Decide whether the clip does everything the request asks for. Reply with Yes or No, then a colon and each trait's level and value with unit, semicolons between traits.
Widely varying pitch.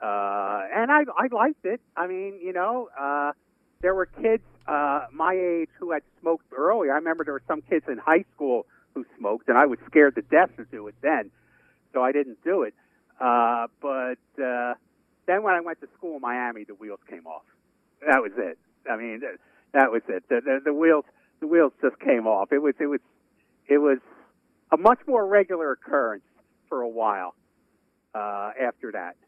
Yes: wide, 6.4 semitones